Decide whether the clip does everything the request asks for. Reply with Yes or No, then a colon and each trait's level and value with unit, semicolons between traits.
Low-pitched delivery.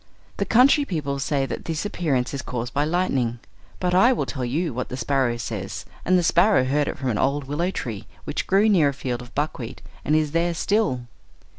No: medium, 145 Hz